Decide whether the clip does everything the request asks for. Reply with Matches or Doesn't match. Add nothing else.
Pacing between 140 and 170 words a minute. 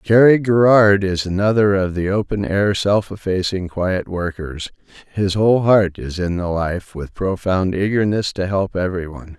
Matches